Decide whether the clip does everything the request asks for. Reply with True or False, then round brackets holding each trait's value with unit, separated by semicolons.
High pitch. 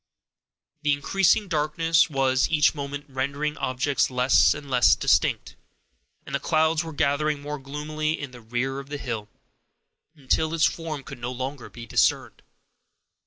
False (145 Hz)